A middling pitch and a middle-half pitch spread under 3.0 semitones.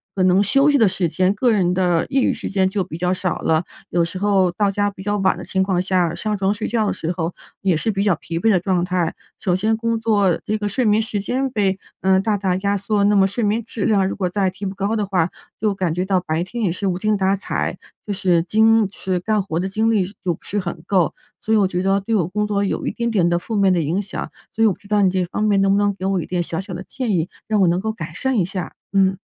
No: high, 195 Hz; narrow, 2.4 semitones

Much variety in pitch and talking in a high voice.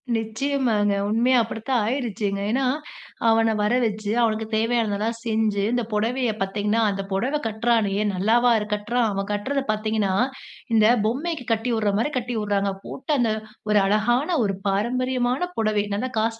No: average, 2.7 semitones; high, 225 Hz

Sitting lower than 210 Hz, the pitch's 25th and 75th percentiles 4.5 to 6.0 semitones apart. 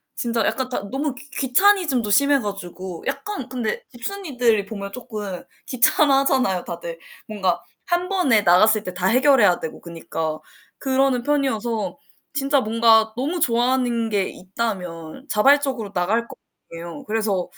No: high, 230 Hz; wide, 5.4 semitones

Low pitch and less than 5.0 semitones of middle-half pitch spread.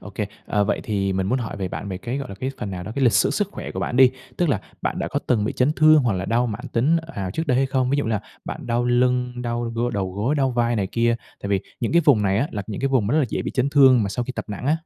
Yes: low, 120 Hz; average, 4.6 semitones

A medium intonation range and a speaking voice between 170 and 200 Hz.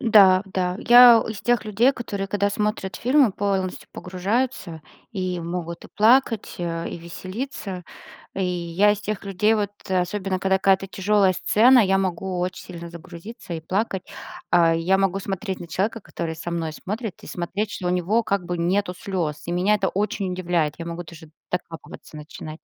Yes: average, 3.1 semitones; high, 190 Hz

